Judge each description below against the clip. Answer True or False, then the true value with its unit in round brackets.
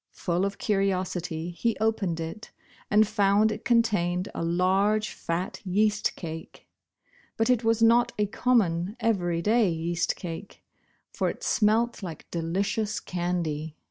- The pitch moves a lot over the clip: False (3.9 semitones)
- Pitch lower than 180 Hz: False (195 Hz)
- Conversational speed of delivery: False (130 wpm)